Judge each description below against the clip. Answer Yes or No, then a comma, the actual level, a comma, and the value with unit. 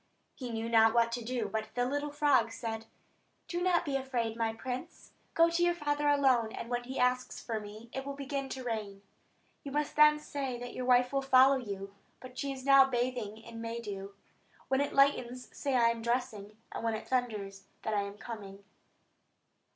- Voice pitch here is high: Yes, high, 245 Hz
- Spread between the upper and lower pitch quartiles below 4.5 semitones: Yes, average, 3.5 semitones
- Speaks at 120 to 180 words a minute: No, fast, 205 wpm